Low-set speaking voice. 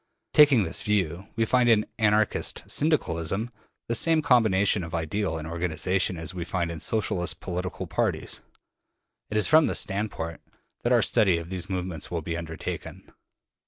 Yes: very low, 95 Hz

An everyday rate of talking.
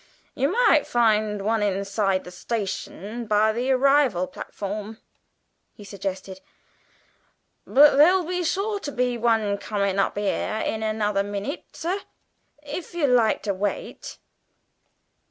No: slow, 125 wpm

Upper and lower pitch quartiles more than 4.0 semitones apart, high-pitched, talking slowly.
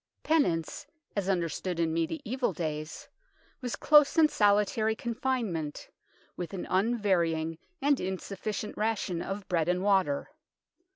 Yes: average, 5.1 semitones; high, 195 Hz; slow, 120 wpm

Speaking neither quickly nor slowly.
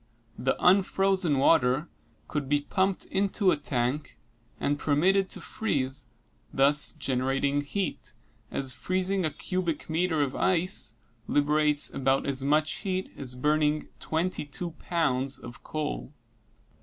No: slow, 125 wpm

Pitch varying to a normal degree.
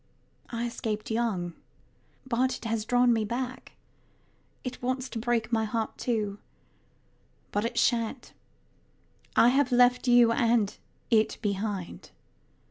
No: narrow, 2.1 semitones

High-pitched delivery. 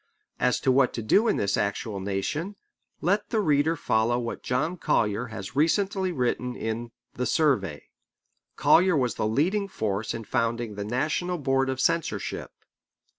No: low, 125 Hz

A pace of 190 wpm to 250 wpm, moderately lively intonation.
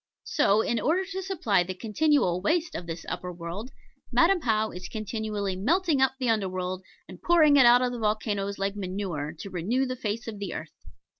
No: average, 200 wpm; wide, 6.1 semitones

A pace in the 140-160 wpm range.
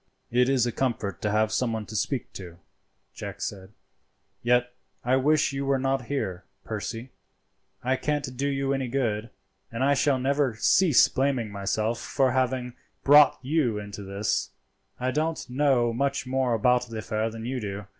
No: average, 170 wpm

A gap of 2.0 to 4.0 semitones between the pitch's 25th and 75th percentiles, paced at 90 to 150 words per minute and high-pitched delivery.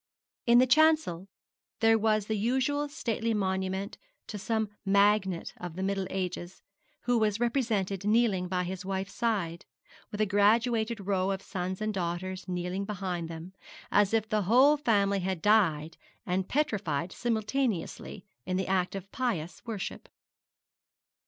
Yes: average, 3.3 semitones; average, 145 wpm; high, 200 Hz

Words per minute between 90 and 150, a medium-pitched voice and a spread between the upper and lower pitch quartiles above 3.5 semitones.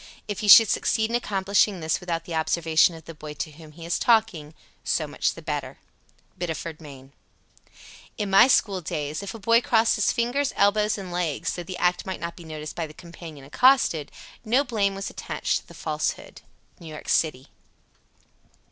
No: average, 190 wpm; medium, 175 Hz; average, 4.9 semitones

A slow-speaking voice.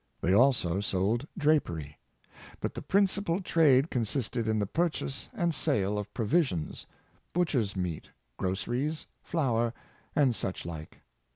Yes: slow, 125 wpm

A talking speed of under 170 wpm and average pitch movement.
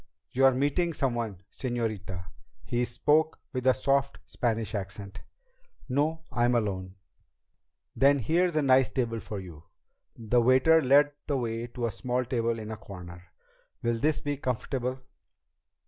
Yes: average, 140 wpm; average, 3.8 semitones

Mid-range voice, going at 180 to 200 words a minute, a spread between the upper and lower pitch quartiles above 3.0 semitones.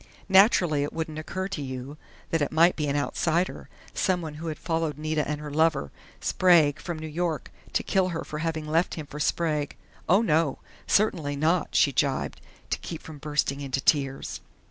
No: medium, 155 Hz; average, 185 wpm; narrow, 2.5 semitones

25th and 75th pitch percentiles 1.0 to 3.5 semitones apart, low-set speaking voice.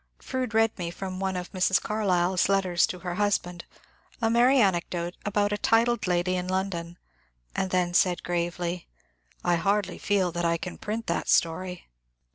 No: average, 2.7 semitones; medium, 185 Hz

